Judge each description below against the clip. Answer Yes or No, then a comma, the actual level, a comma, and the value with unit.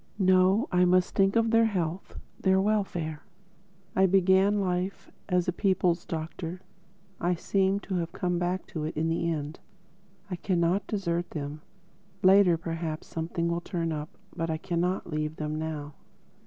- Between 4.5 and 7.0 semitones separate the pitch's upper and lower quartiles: No, average, 2.7 semitones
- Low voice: No, medium, 175 Hz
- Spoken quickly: No, average, 155 wpm